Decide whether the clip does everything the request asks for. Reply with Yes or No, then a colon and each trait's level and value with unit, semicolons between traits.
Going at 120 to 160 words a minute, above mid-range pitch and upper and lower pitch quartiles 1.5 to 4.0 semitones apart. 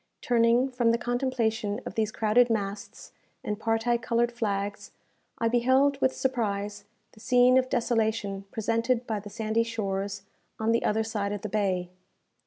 Yes: average, 155 wpm; high, 225 Hz; average, 2.7 semitones